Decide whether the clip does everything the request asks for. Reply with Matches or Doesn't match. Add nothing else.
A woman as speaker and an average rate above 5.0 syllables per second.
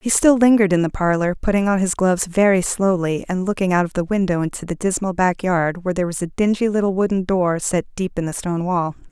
Matches